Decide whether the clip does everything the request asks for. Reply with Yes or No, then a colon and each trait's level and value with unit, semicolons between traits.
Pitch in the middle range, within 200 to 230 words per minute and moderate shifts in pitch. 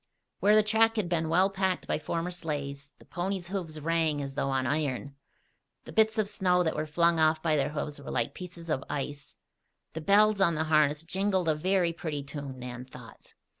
Yes: medium, 160 Hz; fast, 205 wpm; average, 4.2 semitones